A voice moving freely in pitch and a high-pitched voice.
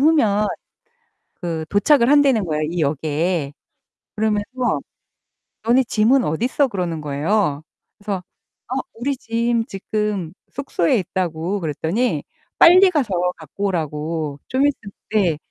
Yes: wide, 6.8 semitones; high, 200 Hz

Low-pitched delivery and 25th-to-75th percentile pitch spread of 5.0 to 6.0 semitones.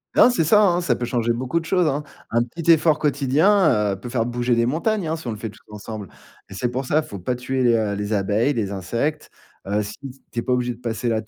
Yes: low, 125 Hz; wide, 5.4 semitones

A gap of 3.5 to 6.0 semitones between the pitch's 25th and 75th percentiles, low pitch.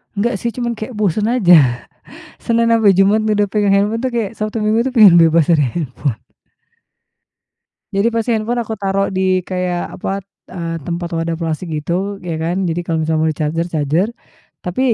No: average, 4.6 semitones; high, 190 Hz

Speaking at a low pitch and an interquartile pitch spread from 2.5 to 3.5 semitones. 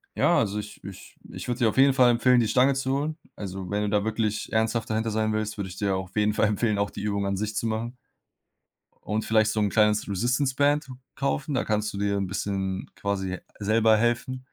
Yes: low, 110 Hz; average, 2.9 semitones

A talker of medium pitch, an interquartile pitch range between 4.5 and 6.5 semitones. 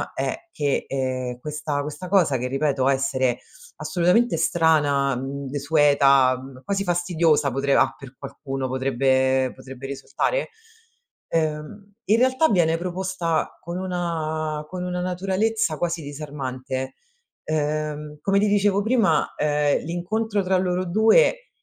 Yes: medium, 155 Hz; average, 5.0 semitones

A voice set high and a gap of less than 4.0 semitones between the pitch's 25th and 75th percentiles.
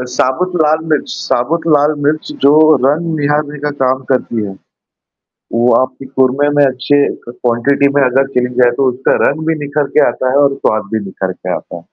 No: low, 135 Hz; average, 2.8 semitones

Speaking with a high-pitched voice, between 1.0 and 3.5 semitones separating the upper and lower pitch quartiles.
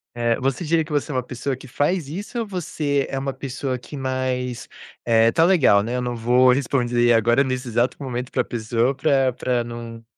No: low, 130 Hz; average, 2.7 semitones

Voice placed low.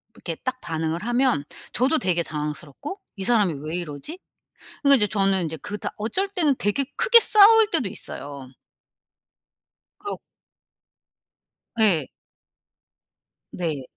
No: high, 205 Hz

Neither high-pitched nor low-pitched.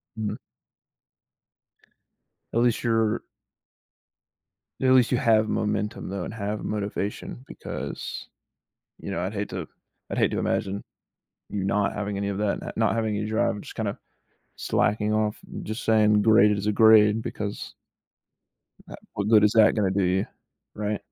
No: low, 105 Hz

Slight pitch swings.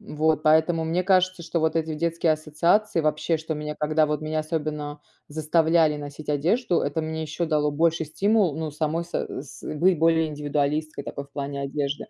Yes: narrow, 1.7 semitones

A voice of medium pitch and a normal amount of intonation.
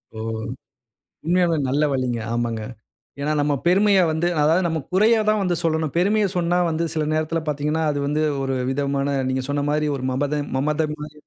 Yes: medium, 150 Hz; average, 3.3 semitones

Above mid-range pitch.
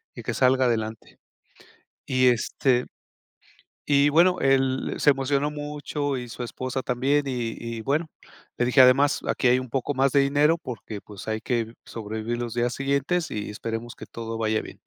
No: low, 130 Hz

